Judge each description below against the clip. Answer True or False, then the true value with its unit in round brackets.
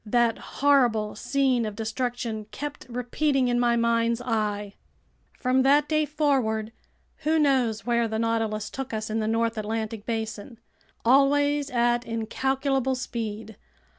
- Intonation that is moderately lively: True (3.3 semitones)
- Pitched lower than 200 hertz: False (235 Hz)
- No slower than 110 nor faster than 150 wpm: True (135 wpm)